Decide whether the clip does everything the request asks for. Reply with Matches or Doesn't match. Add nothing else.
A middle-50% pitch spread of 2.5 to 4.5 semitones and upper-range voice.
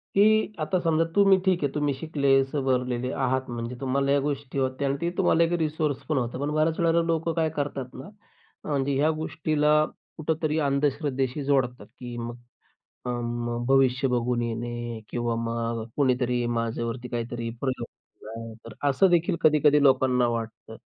Doesn't match